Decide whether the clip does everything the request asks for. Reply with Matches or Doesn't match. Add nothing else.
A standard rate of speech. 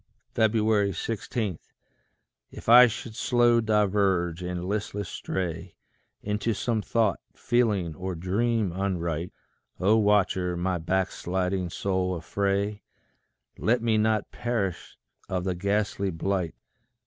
Doesn't match